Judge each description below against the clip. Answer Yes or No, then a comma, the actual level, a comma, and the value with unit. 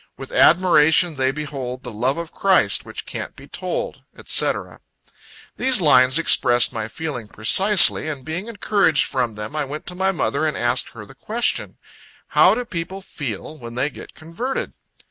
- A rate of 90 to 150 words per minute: No, average, 165 wpm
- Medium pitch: Yes, medium, 155 Hz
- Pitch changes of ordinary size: No, wide, 6.7 semitones